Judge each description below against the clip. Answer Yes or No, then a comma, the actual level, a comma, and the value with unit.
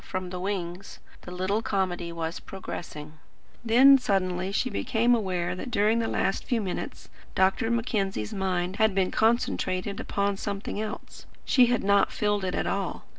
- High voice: Yes, high, 195 Hz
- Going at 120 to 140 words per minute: No, average, 160 wpm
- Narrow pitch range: No, average, 3.2 semitones